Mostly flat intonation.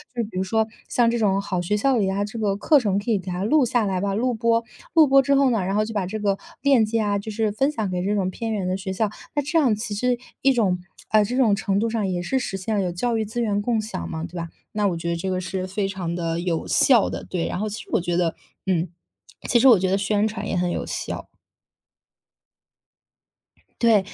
No: average, 3.6 semitones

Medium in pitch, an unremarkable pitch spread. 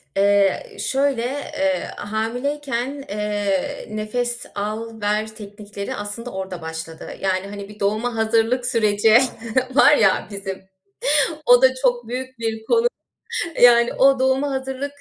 No: high, 225 Hz; average, 4.1 semitones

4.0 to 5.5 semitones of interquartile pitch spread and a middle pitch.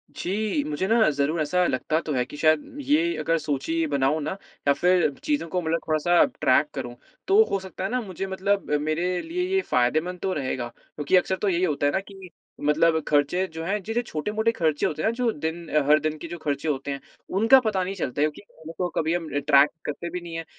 Yes: average, 4.3 semitones; medium, 165 Hz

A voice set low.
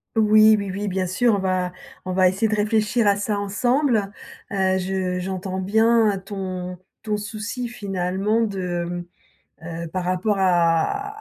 No: high, 195 Hz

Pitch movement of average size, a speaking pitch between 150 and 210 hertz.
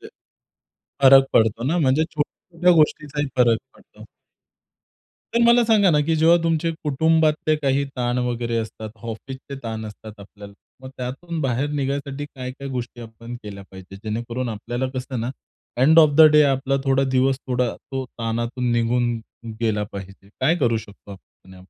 No: average, 4.2 semitones; low, 130 Hz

